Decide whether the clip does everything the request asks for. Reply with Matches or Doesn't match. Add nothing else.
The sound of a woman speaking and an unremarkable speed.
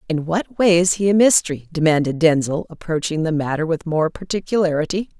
Matches